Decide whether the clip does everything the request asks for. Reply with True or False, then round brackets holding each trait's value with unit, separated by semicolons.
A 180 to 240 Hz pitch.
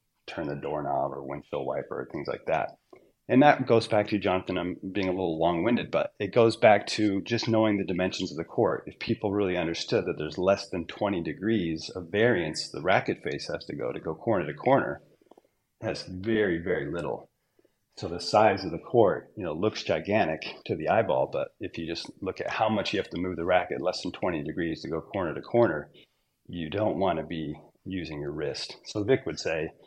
False (95 Hz)